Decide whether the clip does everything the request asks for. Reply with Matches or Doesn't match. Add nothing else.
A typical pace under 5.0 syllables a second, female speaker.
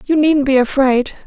Matches